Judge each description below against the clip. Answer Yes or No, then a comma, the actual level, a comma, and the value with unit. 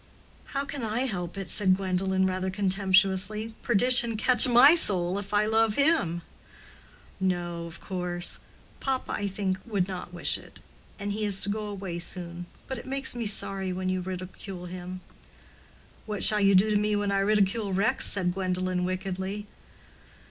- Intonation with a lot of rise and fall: No, narrow, 2.5 semitones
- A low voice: No, high, 195 Hz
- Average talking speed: Yes, average, 165 wpm